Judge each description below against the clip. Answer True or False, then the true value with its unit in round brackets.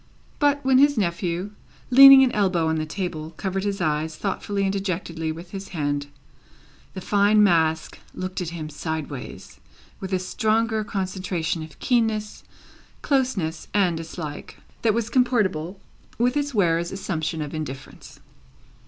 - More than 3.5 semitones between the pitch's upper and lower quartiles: True (4.9 semitones)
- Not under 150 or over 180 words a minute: False (140 wpm)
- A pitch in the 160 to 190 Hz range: True (185 Hz)